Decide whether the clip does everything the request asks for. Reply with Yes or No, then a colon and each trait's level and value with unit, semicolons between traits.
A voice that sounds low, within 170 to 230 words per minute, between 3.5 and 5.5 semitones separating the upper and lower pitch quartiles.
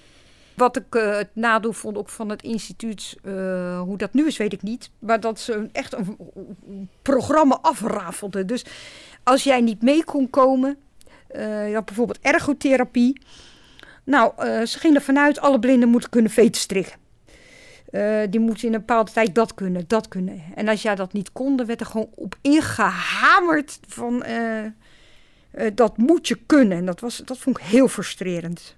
No: high, 225 Hz; average, 180 wpm; average, 3.8 semitones